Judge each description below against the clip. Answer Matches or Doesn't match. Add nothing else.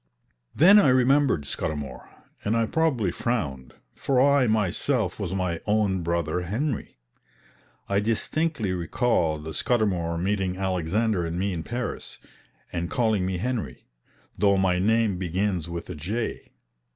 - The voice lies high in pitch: Doesn't match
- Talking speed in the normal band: Doesn't match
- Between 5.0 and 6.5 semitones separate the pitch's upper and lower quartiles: Matches